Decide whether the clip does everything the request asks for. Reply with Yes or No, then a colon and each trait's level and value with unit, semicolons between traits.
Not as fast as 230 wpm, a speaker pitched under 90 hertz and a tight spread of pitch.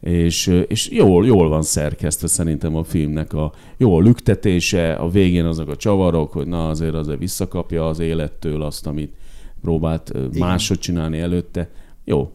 Yes: average, 150 wpm; very low, 80 Hz; narrow, 2.1 semitones